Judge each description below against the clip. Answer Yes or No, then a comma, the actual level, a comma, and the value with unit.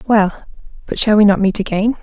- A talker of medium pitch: No, high, 205 Hz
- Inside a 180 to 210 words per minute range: Yes, fast, 205 wpm